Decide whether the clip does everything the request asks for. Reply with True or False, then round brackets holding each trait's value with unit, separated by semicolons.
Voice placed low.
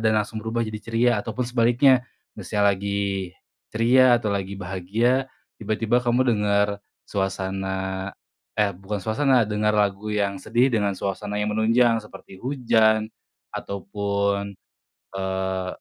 True (105 Hz)